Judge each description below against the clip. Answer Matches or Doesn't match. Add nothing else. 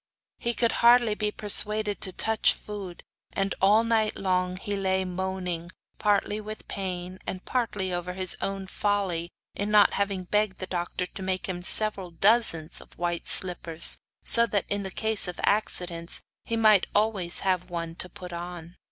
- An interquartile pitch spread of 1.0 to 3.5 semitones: Matches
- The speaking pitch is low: Doesn't match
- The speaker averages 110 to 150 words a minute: Doesn't match